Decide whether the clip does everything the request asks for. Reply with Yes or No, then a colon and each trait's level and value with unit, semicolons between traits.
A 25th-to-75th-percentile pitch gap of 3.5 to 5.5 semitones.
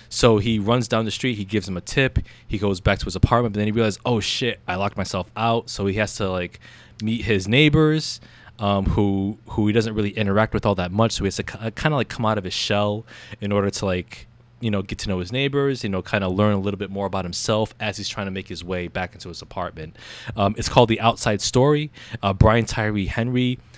No: average, 2.7 semitones